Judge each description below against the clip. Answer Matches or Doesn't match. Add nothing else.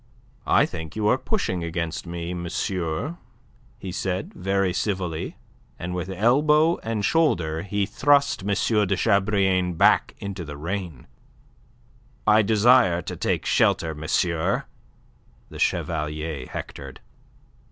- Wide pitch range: Doesn't match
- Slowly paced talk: Matches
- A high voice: Doesn't match